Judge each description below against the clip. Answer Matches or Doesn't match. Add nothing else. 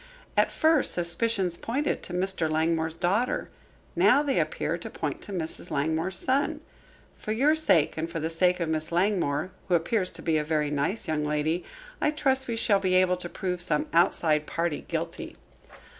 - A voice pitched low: Doesn't match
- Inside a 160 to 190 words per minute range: Matches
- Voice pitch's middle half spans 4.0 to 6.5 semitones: Matches